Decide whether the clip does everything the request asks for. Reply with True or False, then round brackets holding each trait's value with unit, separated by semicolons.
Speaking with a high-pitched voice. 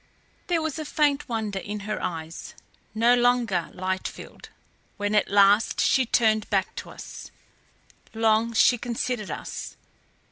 True (220 Hz)